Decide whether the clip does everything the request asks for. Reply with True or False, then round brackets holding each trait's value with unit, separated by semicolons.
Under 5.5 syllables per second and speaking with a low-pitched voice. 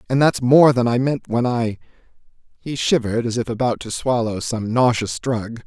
True (5.0 syllables/s; 120 Hz)